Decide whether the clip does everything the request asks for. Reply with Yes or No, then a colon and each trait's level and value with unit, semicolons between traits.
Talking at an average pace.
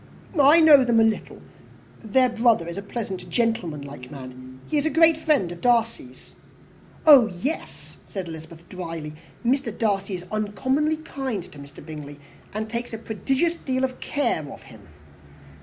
Yes: average, 155 wpm